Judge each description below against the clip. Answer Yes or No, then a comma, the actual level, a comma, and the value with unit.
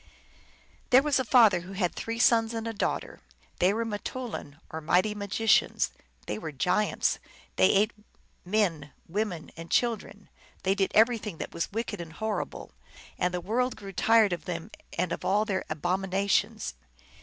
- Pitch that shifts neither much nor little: Yes, average, 4.1 semitones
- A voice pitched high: Yes, high, 200 Hz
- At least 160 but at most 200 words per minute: Yes, average, 165 wpm